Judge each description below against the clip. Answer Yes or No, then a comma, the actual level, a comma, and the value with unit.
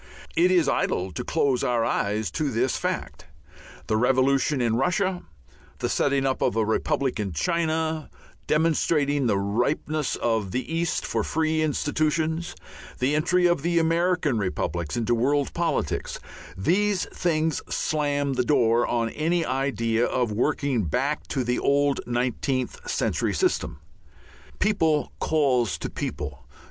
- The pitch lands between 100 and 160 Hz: Yes, medium, 140 Hz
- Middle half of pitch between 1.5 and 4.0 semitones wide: No, average, 5.0 semitones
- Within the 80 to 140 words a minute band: Yes, slow, 135 wpm